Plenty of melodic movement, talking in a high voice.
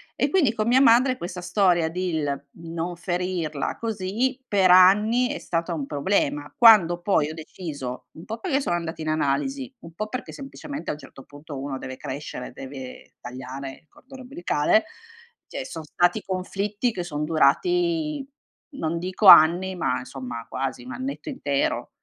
No: wide, 7.5 semitones; medium, 175 Hz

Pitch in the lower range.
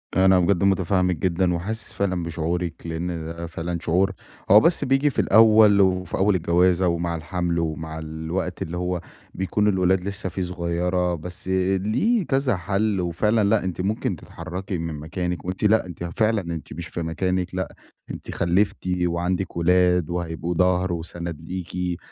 Yes: very low, 90 Hz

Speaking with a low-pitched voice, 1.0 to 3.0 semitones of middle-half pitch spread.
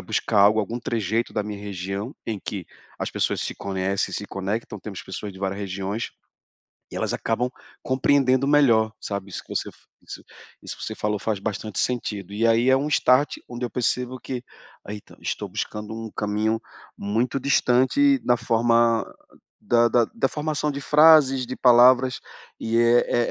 No: low, 115 Hz; average, 3.6 semitones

